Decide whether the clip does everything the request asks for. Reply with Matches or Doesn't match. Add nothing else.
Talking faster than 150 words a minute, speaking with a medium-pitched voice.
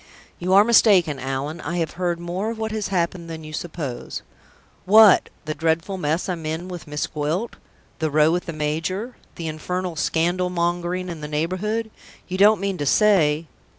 Matches